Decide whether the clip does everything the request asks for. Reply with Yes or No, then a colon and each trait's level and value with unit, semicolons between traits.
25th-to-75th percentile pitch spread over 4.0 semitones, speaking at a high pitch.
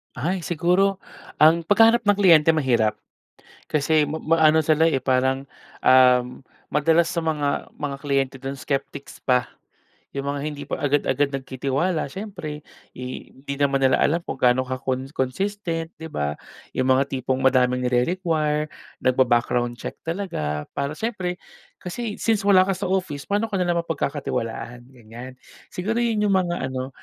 No: average, 5.0 semitones; medium, 145 Hz